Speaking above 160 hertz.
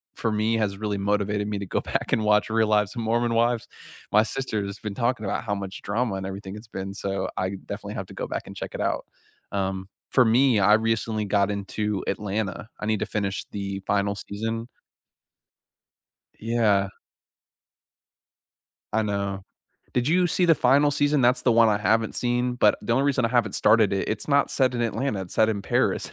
No: low, 110 Hz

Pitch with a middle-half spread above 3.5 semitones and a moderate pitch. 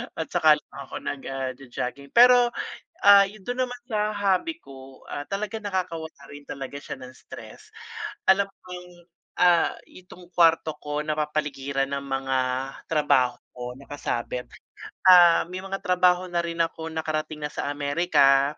Yes: average, 4.8 semitones; medium, 160 Hz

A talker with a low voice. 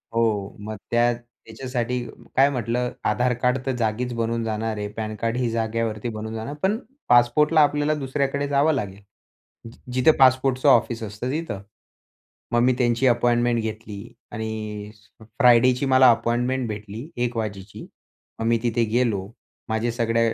Yes: low, 120 Hz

